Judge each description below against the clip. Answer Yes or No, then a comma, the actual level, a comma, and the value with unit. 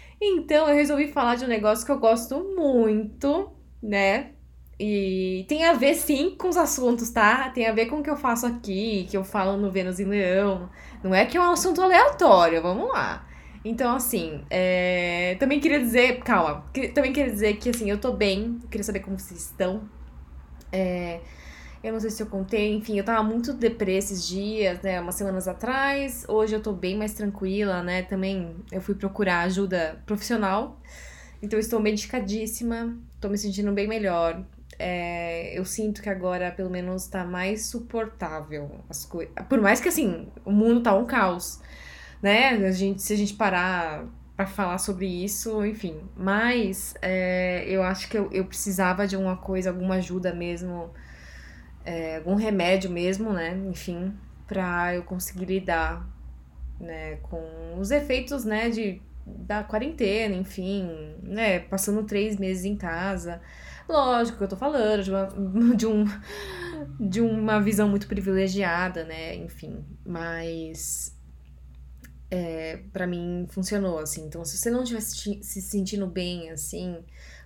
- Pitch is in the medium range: No, high, 195 Hz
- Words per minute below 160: No, average, 165 wpm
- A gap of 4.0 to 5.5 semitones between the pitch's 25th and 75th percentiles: No, average, 3.6 semitones